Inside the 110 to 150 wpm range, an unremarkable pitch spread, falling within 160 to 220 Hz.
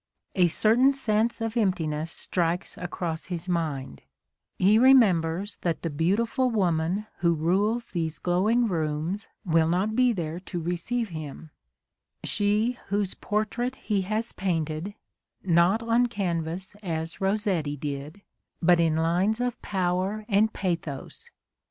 Yes: slow, 135 wpm; average, 4.7 semitones; medium, 185 Hz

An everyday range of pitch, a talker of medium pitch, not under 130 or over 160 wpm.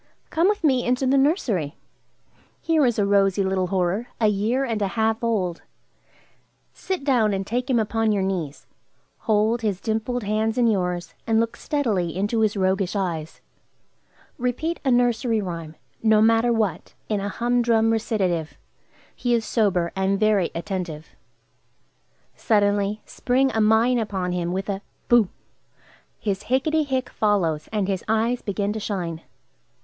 No: average, 3.8 semitones; high, 215 Hz; average, 150 wpm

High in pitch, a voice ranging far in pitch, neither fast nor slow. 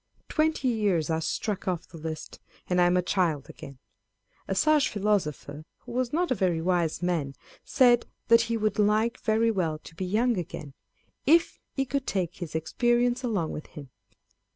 Yes: high, 195 Hz; wide, 6.5 semitones; average, 180 wpm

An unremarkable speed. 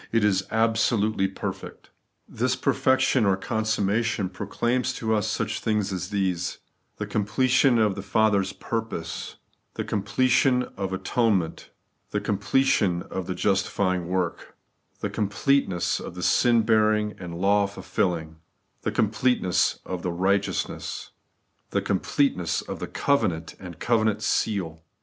No: slow, 130 wpm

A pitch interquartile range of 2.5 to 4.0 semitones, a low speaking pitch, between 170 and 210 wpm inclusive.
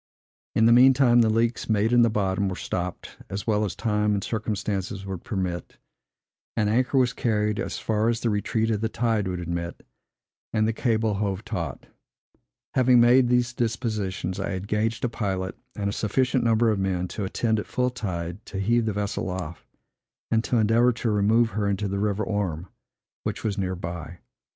Yes: average, 3.1 semitones; low, 105 Hz; average, 190 wpm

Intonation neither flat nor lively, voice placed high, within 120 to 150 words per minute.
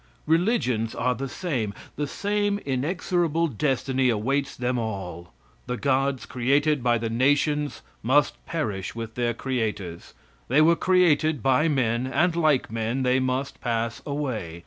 No: average, 4.3 semitones; low, 130 Hz; average, 140 wpm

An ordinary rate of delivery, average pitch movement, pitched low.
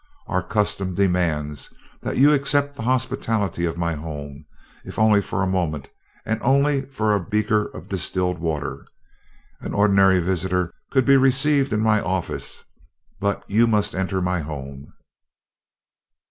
Yes: average, 145 wpm; average, 4.7 semitones; very low, 95 Hz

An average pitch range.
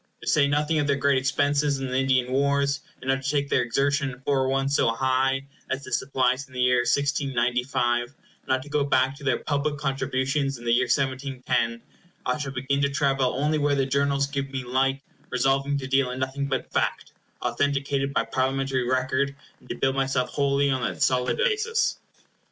No: narrow, 1.5 semitones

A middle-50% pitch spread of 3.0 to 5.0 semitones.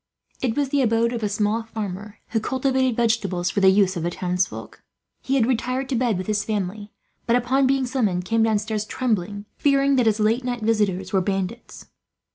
Yes: average, 3.7 semitones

